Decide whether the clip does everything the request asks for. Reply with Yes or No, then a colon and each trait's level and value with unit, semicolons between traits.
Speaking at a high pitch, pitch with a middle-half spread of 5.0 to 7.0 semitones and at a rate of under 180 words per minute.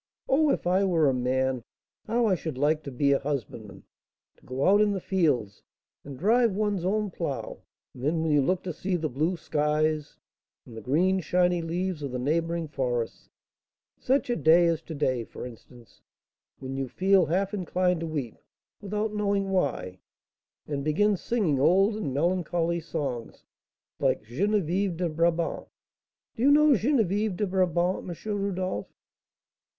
No: medium, 170 Hz; wide, 5.4 semitones; average, 165 wpm